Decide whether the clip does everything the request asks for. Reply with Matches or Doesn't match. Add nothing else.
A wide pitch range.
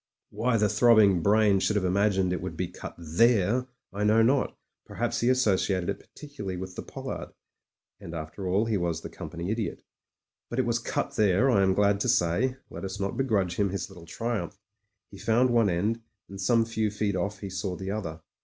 Doesn't match